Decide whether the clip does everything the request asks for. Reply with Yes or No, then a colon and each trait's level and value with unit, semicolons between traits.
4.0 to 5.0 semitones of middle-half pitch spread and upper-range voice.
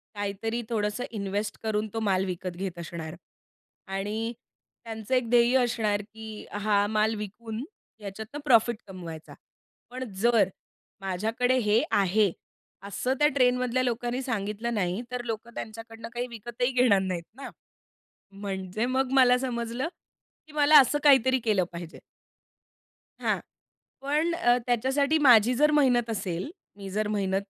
No: average, 3.6 semitones; high, 225 Hz